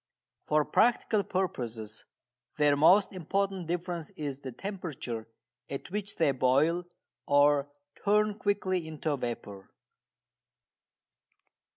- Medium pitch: Yes, medium, 160 Hz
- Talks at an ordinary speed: No, slow, 95 wpm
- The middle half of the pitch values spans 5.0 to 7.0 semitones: Yes, wide, 5.6 semitones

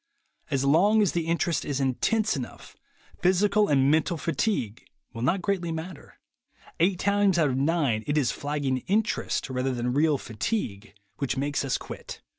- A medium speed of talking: Yes, average, 160 wpm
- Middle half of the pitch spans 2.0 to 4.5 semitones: No, wide, 5.6 semitones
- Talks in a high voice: No, medium, 150 Hz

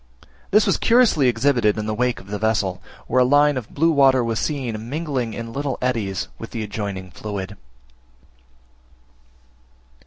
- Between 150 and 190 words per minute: Yes, average, 155 wpm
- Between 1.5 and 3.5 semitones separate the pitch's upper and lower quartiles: No, average, 4.8 semitones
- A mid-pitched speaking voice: No, low, 120 Hz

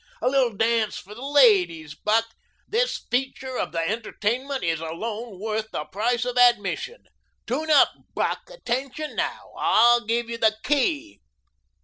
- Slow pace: No, average, 145 wpm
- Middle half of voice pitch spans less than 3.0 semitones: No, average, 3.8 semitones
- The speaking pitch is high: Yes, high, 235 Hz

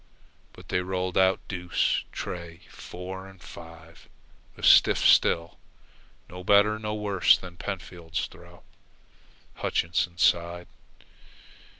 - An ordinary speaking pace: No, slow, 110 wpm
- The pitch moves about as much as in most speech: No, narrow, 1.8 semitones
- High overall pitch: No, very low, 90 Hz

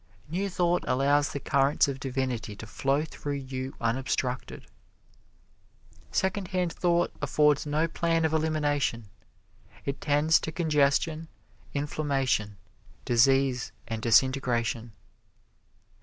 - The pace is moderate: No, slow, 100 wpm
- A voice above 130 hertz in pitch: Yes, medium, 140 Hz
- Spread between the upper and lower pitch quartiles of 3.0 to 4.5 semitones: Yes, average, 3.4 semitones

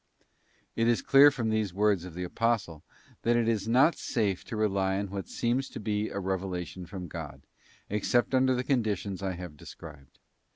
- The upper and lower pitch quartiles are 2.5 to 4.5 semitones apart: Yes, average, 4.1 semitones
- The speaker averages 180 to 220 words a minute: Yes, average, 190 wpm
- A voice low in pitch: Yes, low, 105 Hz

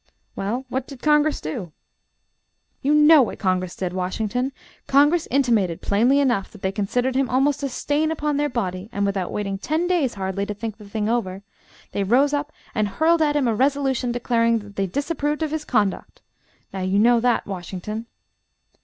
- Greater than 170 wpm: Yes, average, 180 wpm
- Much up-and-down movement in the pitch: Yes, wide, 6.2 semitones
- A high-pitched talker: Yes, high, 240 Hz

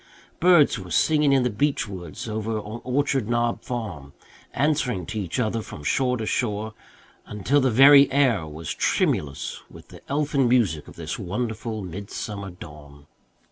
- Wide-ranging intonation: Yes, wide, 5.7 semitones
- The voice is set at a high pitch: No, low, 110 Hz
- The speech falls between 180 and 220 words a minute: No, average, 155 wpm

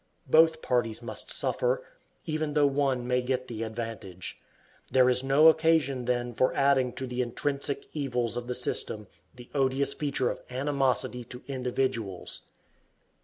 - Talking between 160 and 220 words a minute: No, average, 145 wpm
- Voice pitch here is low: Yes, low, 130 Hz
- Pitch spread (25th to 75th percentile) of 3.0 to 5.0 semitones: No, narrow, 2.5 semitones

